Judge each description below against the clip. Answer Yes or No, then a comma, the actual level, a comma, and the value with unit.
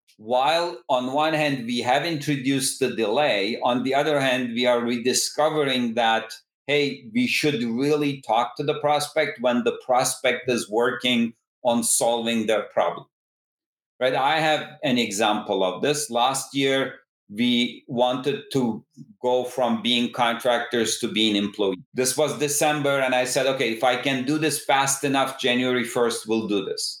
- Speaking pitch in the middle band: No, low, 130 Hz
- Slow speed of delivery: No, average, 160 wpm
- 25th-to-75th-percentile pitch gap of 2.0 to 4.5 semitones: Yes, average, 3.6 semitones